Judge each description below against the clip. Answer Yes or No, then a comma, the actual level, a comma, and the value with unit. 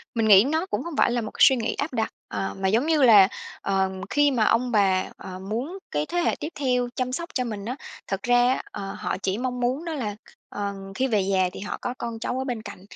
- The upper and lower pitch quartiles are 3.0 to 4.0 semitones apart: No, average, 4.5 semitones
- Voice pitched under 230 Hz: No, high, 235 Hz